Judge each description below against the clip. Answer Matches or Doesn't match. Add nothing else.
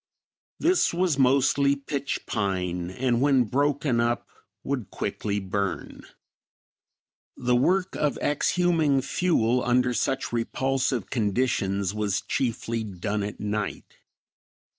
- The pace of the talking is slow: Matches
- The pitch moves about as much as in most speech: Matches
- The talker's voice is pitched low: Matches